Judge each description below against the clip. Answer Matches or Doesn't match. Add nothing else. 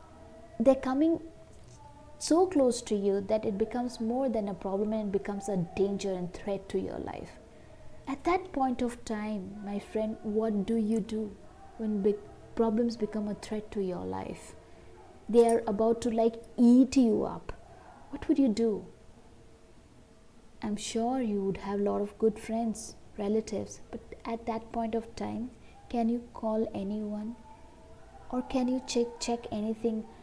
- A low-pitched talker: Doesn't match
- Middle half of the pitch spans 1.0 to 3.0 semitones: Matches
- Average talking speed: Matches